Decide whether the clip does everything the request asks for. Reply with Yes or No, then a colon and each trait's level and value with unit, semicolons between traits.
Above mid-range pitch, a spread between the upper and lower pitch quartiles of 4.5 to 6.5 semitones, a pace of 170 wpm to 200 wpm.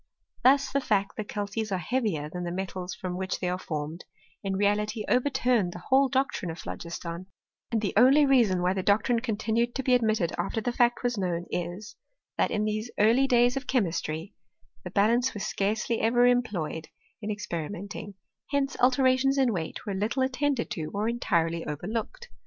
Yes: high, 215 Hz; average, 5.1 semitones; average, 180 wpm